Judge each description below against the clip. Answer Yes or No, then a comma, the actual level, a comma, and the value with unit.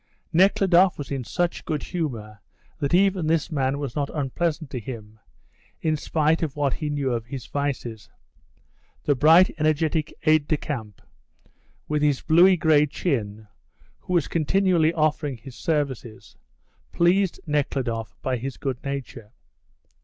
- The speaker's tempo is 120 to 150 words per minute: Yes, average, 140 wpm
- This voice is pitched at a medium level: Yes, medium, 145 Hz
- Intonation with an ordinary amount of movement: Yes, average, 3.7 semitones